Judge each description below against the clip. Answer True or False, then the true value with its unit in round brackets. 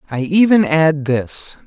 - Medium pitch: True (155 Hz)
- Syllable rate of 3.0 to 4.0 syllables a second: True (3.6 syllables/s)